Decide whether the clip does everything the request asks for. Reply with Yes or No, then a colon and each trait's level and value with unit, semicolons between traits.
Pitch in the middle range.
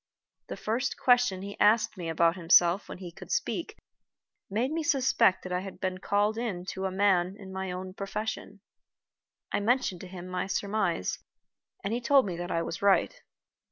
No: high, 195 Hz